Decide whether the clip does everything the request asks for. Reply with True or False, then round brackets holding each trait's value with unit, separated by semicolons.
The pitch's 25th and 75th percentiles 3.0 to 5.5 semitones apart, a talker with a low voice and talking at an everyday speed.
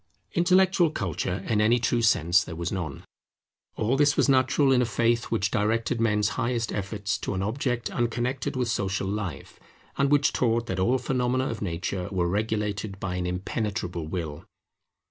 True (4.5 semitones; 110 Hz; 170 wpm)